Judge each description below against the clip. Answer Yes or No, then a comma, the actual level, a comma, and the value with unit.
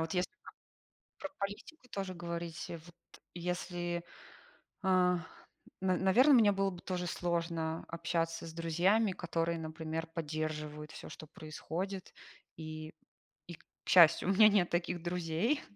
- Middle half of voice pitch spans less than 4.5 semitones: Yes, narrow, 2.4 semitones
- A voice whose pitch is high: No, medium, 175 Hz